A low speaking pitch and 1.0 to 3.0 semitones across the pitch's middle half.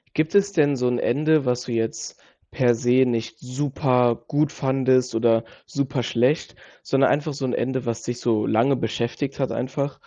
Yes: low, 130 Hz; average, 2.7 semitones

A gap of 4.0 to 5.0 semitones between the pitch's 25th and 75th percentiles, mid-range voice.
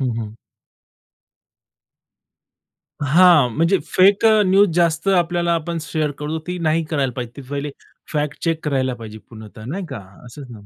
Yes: average, 4.7 semitones; medium, 155 Hz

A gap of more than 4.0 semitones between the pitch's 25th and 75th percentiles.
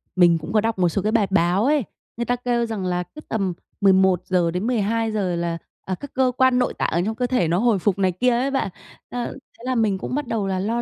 Yes: average, 4.9 semitones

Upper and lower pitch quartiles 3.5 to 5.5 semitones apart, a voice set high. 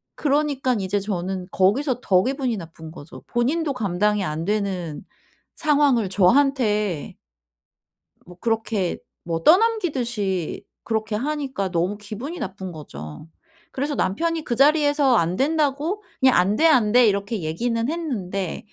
No: wide, 7.0 semitones; high, 220 Hz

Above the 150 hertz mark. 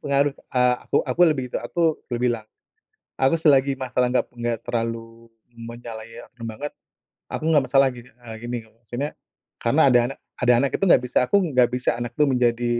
No: low, 125 Hz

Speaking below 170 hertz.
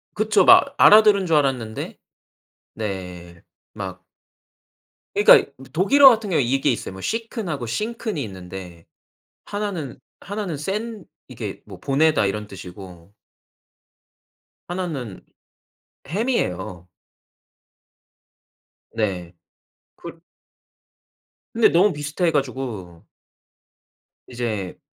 Yes: medium, 140 Hz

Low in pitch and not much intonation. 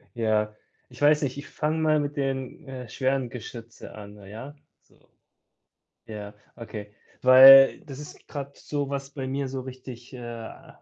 No: low, 130 Hz; average, 3.3 semitones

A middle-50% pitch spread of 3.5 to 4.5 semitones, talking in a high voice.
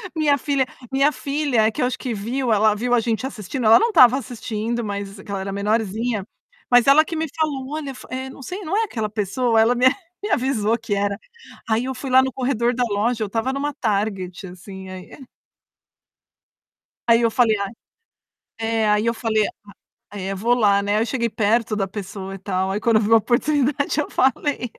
Yes: average, 4.1 semitones; high, 230 Hz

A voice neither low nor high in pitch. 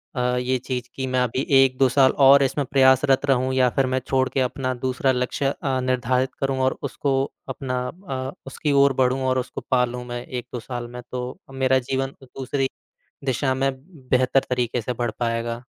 No: low, 130 Hz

